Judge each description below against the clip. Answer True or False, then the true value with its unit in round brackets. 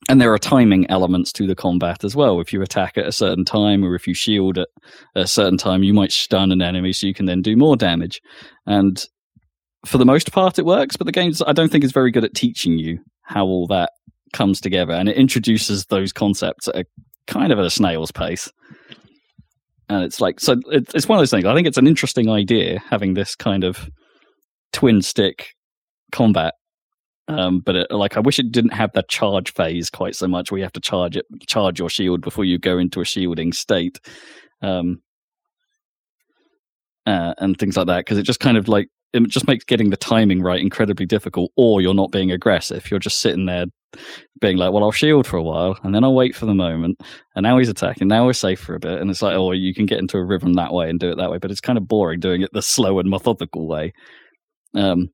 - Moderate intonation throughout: True (4.0 semitones)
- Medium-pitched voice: False (95 Hz)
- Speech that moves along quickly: True (230 wpm)